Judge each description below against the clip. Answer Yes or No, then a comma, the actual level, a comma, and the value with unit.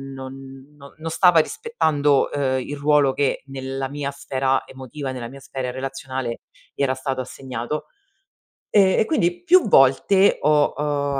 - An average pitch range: No, narrow, 2.1 semitones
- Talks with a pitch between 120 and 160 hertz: Yes, medium, 140 Hz